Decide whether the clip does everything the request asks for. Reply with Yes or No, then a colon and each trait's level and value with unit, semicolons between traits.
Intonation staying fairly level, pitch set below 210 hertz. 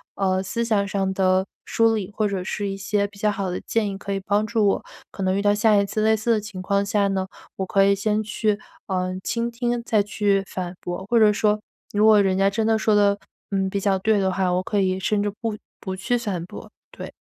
Yes: narrow, 1.9 semitones; high, 200 Hz